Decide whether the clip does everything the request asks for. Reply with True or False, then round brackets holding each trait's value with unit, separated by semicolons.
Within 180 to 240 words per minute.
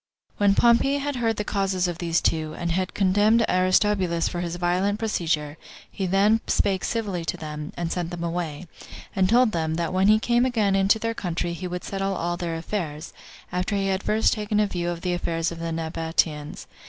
True (205 wpm)